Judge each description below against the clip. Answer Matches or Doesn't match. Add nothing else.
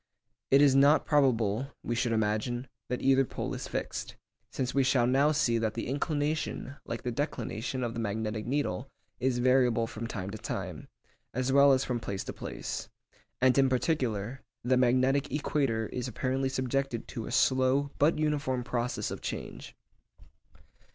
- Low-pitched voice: Matches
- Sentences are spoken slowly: Doesn't match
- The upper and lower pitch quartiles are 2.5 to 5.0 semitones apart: Matches